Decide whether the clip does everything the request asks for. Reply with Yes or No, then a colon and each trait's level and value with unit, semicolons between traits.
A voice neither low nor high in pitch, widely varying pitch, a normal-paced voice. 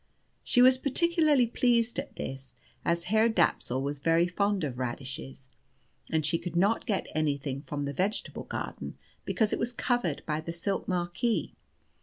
Yes: medium, 175 Hz; wide, 7.9 semitones; average, 160 wpm